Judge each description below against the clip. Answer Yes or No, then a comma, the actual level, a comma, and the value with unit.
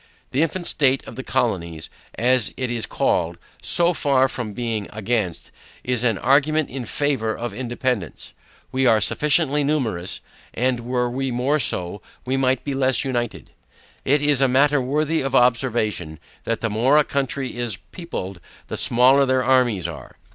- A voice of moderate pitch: No, low, 125 Hz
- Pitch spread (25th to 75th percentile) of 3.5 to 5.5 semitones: No, average, 3.1 semitones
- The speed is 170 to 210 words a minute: No, average, 160 wpm